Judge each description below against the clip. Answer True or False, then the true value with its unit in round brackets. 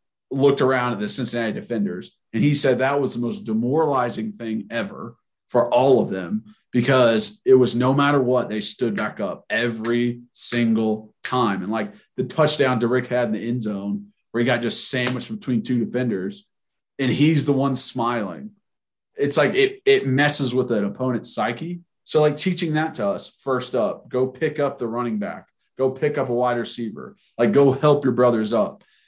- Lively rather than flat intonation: False (3.3 semitones)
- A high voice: False (125 Hz)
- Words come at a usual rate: True (190 wpm)